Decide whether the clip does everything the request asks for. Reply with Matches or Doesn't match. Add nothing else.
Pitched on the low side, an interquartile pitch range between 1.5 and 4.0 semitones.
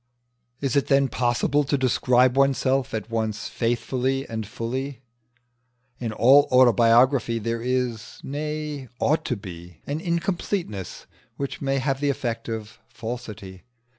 Matches